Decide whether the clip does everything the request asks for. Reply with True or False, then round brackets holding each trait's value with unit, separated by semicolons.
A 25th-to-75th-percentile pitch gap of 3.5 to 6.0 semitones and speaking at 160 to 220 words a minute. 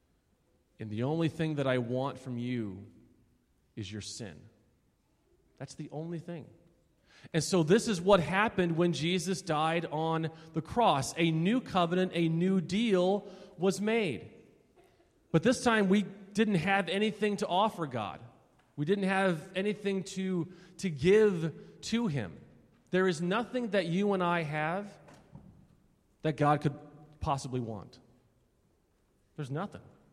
False (5.1 semitones; 140 wpm)